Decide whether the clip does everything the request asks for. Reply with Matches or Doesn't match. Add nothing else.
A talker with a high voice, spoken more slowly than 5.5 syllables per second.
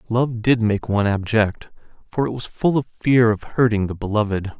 Doesn't match